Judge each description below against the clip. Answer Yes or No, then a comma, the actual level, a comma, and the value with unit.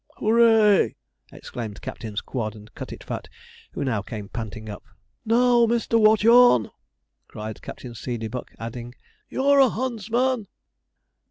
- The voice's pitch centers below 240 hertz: Yes, medium, 140 Hz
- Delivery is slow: Yes, slow, 115 wpm